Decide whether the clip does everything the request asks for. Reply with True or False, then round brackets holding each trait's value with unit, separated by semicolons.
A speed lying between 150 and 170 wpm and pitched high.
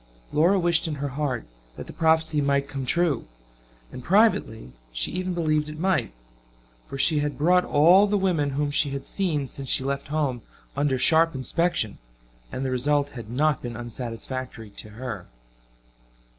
False (165 wpm; 145 Hz)